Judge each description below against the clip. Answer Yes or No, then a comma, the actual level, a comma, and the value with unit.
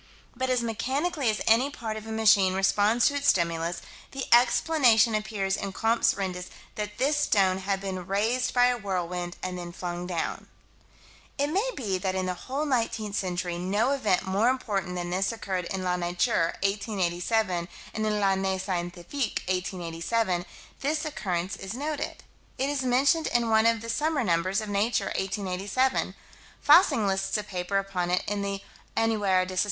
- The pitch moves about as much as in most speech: Yes, average, 4.3 semitones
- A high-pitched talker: Yes, high, 200 Hz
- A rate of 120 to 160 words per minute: No, average, 170 wpm